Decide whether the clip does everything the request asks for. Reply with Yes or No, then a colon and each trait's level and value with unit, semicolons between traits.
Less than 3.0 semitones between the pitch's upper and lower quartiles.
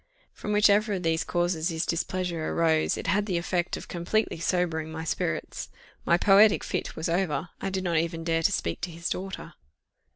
Yes: narrow, 2.6 semitones